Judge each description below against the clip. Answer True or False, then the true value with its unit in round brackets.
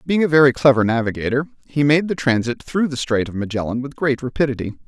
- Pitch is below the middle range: True (130 Hz)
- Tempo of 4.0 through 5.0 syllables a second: False (6.3 syllables/s)